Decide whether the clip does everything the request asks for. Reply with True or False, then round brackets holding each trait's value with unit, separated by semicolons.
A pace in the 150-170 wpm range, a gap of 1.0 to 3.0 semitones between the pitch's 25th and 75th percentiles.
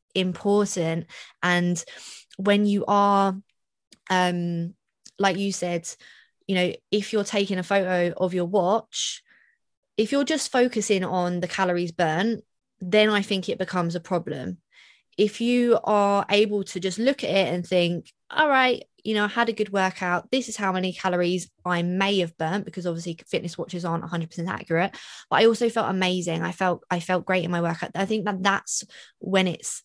False (180 wpm; 2.7 semitones)